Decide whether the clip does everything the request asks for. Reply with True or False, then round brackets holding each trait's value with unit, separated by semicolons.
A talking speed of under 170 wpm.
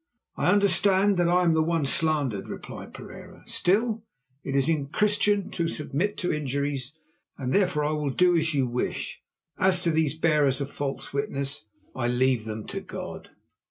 True (160 wpm)